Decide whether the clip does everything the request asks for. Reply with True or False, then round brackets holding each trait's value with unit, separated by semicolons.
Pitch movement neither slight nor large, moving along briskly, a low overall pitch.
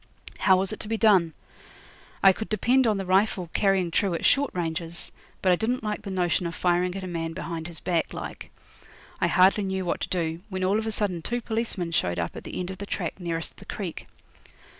False (3.4 semitones; 225 wpm; 185 Hz)